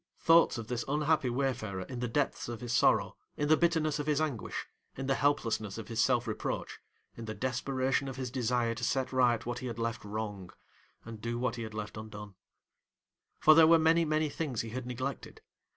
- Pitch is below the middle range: Yes, low, 125 Hz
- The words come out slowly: No, fast, 205 wpm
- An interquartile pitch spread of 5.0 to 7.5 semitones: No, average, 3.9 semitones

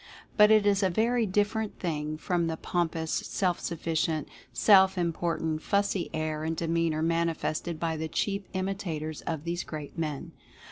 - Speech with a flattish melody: No, average, 3.3 semitones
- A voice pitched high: No, medium, 170 Hz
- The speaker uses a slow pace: No, average, 150 wpm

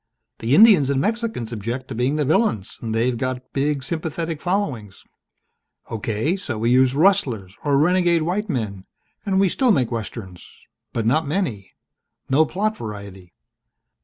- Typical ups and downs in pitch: No, wide, 7.4 semitones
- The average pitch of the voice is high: No, low, 135 Hz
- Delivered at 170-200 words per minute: No, average, 150 wpm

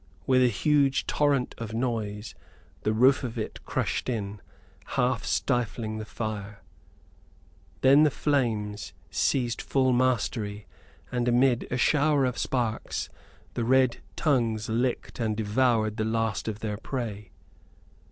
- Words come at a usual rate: No, slow, 130 wpm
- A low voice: Yes, low, 115 Hz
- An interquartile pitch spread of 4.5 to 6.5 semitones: No, average, 3.1 semitones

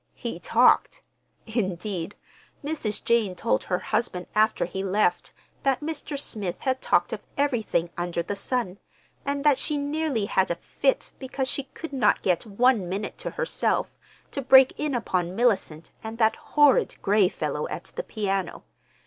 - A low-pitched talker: No, high, 220 Hz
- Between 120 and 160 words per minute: Yes, average, 155 wpm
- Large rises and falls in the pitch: Yes, wide, 6.2 semitones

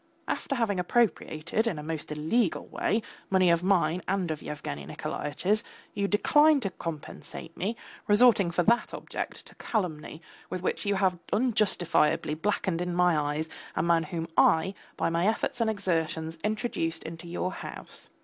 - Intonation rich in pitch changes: No, average, 4.4 semitones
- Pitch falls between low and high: Yes, medium, 180 Hz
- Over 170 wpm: No, average, 160 wpm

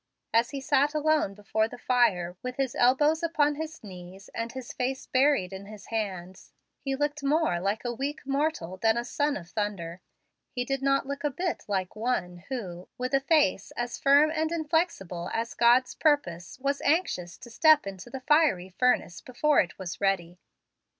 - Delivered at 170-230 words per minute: Yes, average, 175 wpm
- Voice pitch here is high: Yes, high, 245 Hz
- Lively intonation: Yes, wide, 7.0 semitones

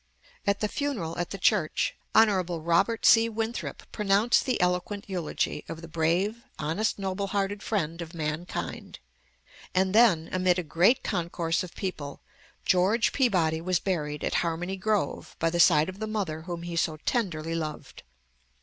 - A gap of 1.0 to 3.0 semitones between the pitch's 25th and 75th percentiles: No, average, 3.8 semitones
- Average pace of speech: Yes, average, 160 wpm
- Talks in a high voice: No, medium, 180 Hz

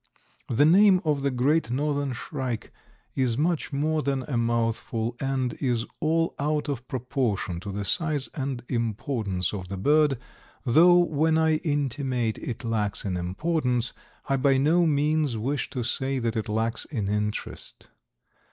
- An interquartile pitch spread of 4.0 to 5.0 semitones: Yes, average, 4.7 semitones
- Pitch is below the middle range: Yes, low, 130 Hz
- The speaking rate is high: No, average, 150 wpm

